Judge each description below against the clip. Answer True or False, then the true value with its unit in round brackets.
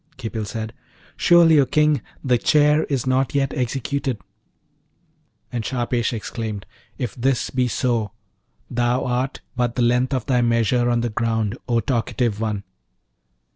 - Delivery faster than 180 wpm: False (140 wpm)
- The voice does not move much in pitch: True (2.3 semitones)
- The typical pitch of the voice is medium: False (120 Hz)